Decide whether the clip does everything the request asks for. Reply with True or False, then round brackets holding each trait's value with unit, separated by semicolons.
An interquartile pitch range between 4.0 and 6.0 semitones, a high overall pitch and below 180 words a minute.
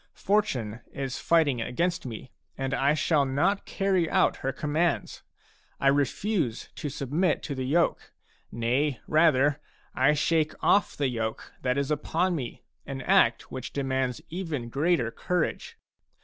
False (4.3 semitones; 140 Hz; 145 wpm)